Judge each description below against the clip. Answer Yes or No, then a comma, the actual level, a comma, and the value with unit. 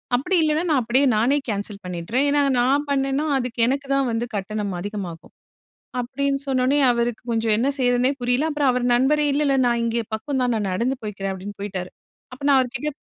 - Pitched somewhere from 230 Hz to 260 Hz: Yes, high, 245 Hz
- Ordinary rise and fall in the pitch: Yes, average, 4.3 semitones